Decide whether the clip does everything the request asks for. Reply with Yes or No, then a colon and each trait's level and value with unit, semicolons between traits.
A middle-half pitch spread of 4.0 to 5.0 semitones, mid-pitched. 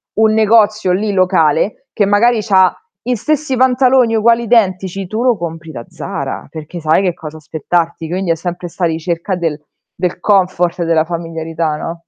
Yes: average, 4.7 semitones; medium, 180 Hz